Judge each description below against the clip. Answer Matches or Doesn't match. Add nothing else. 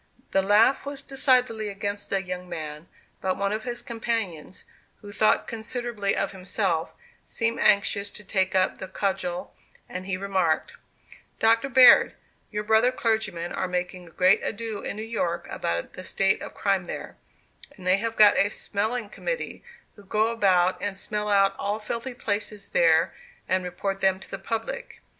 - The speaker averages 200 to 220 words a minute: Doesn't match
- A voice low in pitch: Doesn't match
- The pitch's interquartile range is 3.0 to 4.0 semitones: Matches